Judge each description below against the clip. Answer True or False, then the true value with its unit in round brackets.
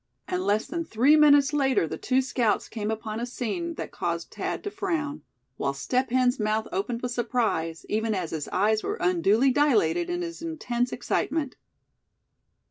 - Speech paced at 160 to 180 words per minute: True (170 wpm)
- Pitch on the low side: False (245 Hz)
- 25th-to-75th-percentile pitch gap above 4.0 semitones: True (5.4 semitones)